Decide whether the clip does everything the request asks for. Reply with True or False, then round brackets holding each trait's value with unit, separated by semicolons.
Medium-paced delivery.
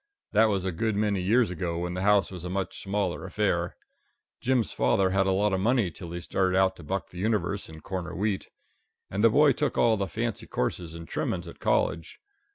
False (215 wpm)